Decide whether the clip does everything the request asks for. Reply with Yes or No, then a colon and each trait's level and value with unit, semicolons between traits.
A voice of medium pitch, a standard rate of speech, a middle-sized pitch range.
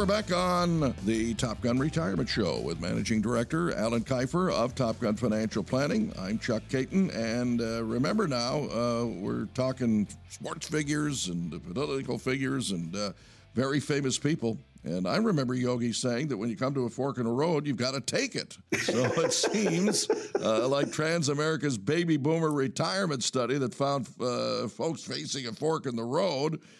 No: low, 130 Hz; average, 175 wpm; average, 4.5 semitones